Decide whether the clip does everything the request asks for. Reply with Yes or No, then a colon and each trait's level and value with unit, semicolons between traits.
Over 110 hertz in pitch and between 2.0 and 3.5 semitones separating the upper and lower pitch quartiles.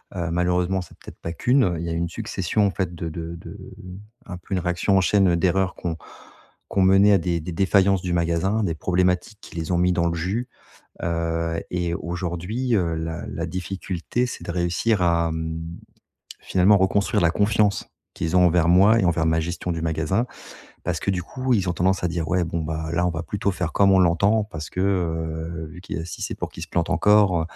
No: very low, 90 Hz; narrow, 2.5 semitones